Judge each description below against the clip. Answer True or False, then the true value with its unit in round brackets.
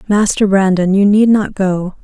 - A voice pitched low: False (195 Hz)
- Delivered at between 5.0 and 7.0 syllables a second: False (4.3 syllables/s)